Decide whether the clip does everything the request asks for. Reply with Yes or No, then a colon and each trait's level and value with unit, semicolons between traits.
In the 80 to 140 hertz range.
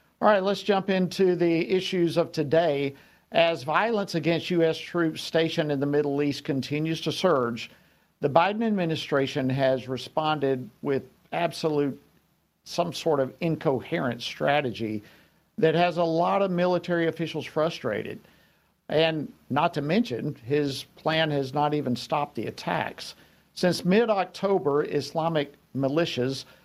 No: medium, 160 Hz